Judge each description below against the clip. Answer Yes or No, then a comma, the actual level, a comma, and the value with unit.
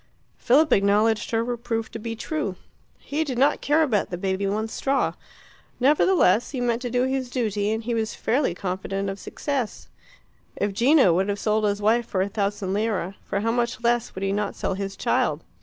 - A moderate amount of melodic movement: Yes, average, 3.6 semitones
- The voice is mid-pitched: No, high, 220 Hz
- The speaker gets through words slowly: No, average, 195 wpm